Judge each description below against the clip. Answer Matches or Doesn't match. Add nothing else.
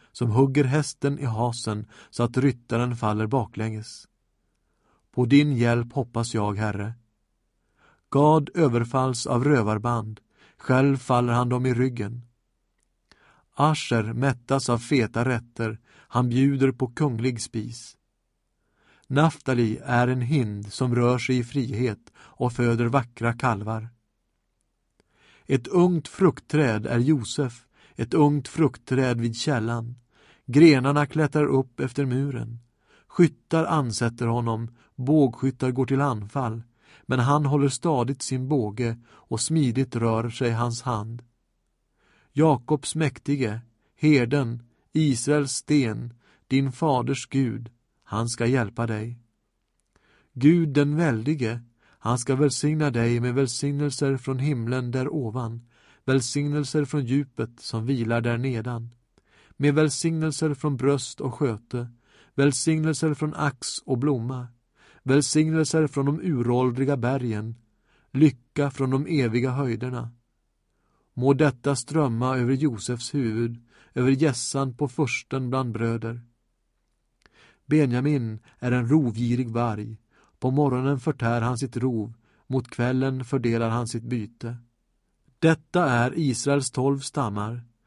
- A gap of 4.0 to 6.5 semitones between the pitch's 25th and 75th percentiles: Doesn't match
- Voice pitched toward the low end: Matches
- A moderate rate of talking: Doesn't match